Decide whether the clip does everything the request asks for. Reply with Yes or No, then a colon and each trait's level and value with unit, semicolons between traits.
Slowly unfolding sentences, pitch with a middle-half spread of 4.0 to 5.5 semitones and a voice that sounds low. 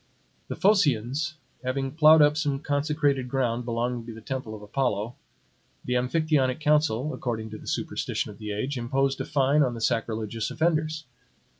No: average, 160 wpm; average, 4.3 semitones; low, 130 Hz